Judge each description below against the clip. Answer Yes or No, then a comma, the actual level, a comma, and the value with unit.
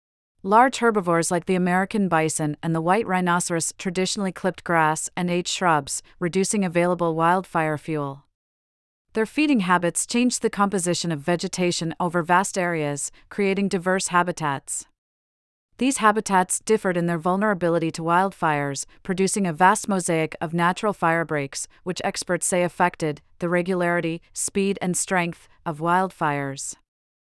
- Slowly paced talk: Yes, slow, 130 wpm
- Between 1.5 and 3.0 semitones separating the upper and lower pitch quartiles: Yes, narrow, 2.6 semitones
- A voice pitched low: No, medium, 175 Hz